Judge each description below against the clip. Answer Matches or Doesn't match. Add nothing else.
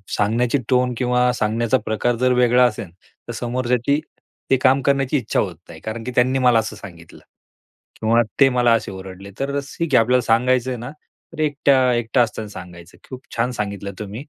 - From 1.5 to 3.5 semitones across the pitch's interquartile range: Matches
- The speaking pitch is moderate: Doesn't match